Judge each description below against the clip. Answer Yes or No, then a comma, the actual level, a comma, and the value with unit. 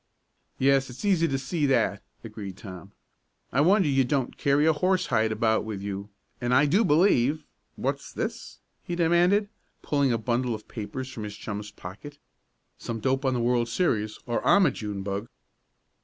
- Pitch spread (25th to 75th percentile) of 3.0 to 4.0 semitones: No, wide, 5.4 semitones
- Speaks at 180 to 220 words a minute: No, average, 170 wpm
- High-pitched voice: No, low, 125 Hz